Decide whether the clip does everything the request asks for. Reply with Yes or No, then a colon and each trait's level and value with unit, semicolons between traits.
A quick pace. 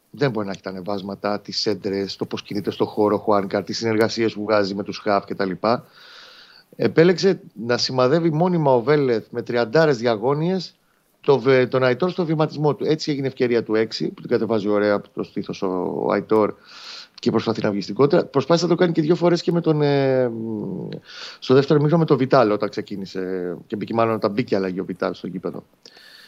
Yes: fast, 195 wpm